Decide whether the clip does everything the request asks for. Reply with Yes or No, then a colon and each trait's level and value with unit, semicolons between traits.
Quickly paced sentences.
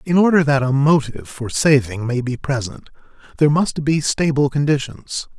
No: average, 165 wpm